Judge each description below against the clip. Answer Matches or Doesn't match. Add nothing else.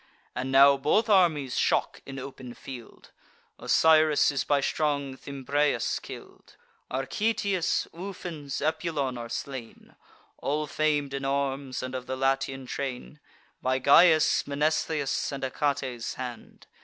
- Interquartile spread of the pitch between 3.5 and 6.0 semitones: Doesn't match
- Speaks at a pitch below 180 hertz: Matches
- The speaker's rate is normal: Doesn't match